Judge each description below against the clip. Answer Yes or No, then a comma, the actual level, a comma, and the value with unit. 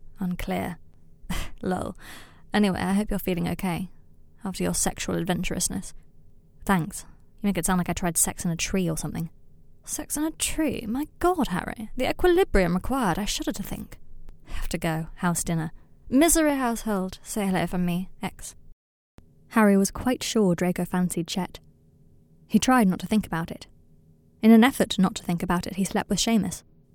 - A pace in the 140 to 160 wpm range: No, average, 175 wpm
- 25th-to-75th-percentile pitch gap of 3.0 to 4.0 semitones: No, average, 4.4 semitones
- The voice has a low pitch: No, medium, 185 Hz